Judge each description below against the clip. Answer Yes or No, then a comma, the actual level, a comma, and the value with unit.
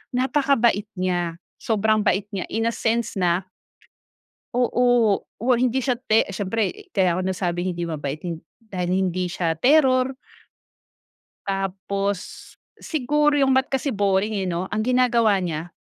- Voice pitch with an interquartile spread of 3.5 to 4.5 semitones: No, average, 5.3 semitones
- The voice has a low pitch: No, high, 205 Hz